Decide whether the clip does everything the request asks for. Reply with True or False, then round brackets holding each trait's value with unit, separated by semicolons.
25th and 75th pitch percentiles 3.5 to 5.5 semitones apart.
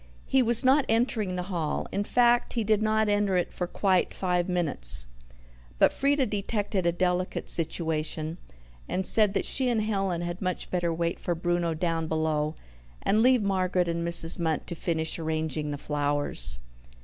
True (4.2 semitones)